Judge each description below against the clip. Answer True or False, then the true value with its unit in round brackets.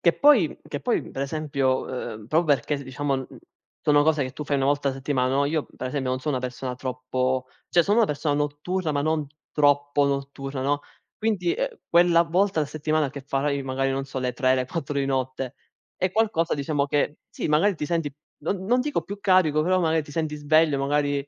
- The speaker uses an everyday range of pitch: True (3.2 semitones)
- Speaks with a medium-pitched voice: True (145 Hz)